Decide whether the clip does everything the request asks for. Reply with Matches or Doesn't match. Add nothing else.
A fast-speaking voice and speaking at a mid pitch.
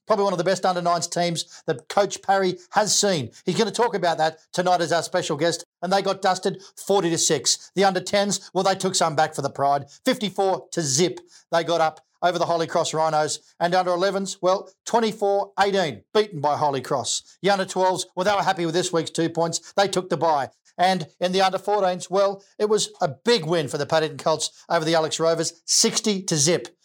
Matches